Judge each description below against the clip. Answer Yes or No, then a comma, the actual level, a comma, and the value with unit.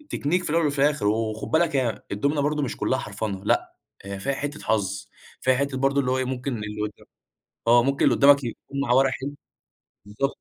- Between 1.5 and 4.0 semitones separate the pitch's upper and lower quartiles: No, average, 4.6 semitones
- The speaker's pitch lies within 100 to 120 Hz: No, low, 130 Hz